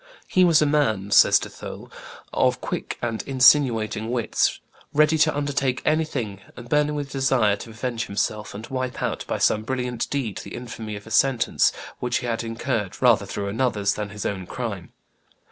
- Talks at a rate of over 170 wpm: Yes, average, 180 wpm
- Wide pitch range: No, average, 4.1 semitones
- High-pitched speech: No, low, 120 Hz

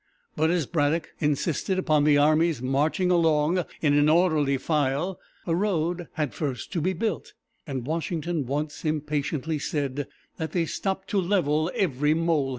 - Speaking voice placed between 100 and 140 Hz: No, medium, 155 Hz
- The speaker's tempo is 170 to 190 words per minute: No, average, 155 wpm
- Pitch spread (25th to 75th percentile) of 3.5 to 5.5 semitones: No, average, 2.9 semitones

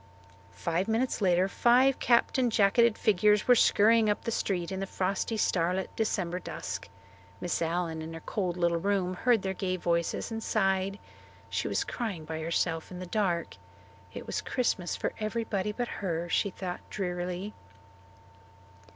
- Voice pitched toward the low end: No, high, 190 Hz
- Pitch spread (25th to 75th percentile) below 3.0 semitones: No, average, 3.7 semitones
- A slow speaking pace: No, average, 160 wpm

